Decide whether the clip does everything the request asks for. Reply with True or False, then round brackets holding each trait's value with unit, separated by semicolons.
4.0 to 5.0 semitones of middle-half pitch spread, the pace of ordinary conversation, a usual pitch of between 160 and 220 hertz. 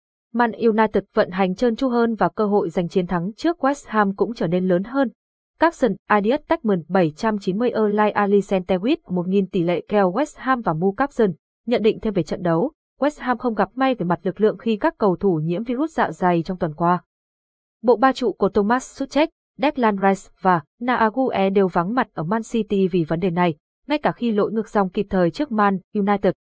True (4.5 semitones; 210 wpm; 210 Hz)